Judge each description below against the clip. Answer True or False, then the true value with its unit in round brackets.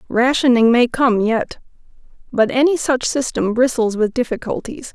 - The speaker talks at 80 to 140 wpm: True (135 wpm)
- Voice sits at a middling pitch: False (245 Hz)